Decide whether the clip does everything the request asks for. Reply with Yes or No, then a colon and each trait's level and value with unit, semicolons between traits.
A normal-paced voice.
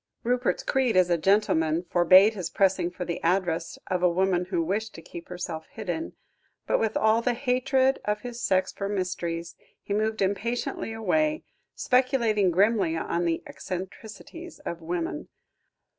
Yes: average, 155 wpm